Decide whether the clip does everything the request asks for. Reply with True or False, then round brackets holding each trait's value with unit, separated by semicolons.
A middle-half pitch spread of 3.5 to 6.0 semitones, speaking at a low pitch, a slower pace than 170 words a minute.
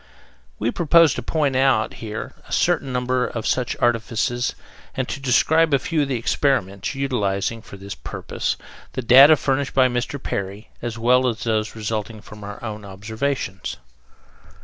True (3.8 semitones; 120 Hz; 160 wpm)